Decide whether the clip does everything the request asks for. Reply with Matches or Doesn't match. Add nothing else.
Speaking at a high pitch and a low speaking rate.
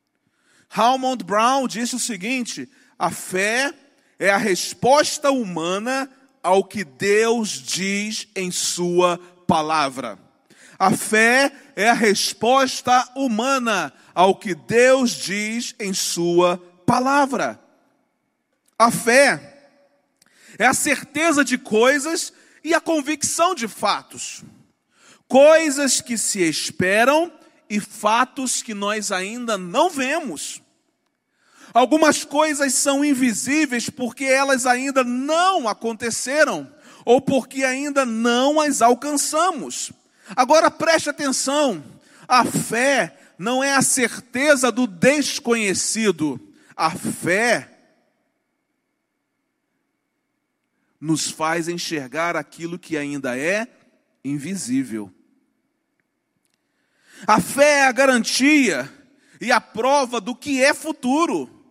Matches